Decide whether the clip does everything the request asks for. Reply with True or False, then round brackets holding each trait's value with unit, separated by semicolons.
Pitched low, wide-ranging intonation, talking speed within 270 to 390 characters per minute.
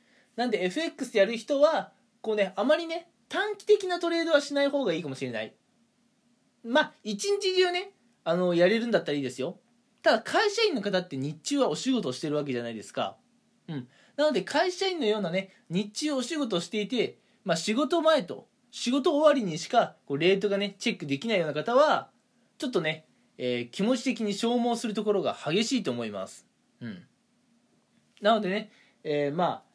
False (235 Hz; 7.1 semitones; 370 characters per minute)